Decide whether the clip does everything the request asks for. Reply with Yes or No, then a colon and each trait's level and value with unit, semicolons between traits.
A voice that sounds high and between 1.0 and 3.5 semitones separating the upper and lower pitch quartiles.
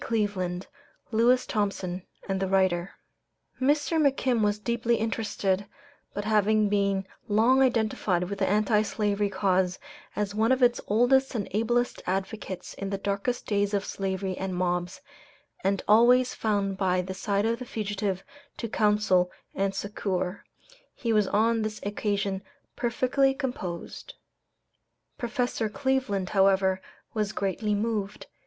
Yes: high, 205 Hz; average, 3.0 semitones